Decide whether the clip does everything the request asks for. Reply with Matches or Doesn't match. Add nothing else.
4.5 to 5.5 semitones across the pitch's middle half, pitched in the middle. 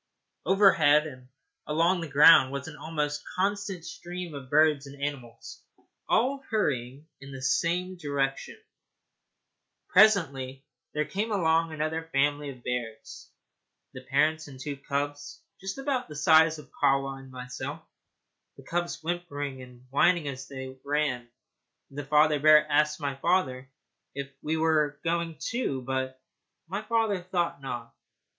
Doesn't match